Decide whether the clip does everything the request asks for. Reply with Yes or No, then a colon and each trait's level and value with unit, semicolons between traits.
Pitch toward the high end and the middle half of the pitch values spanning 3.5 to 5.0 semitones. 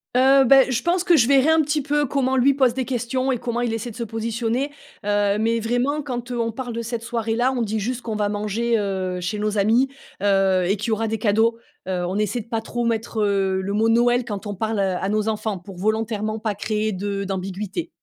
No: high, 225 Hz; average, 3.0 semitones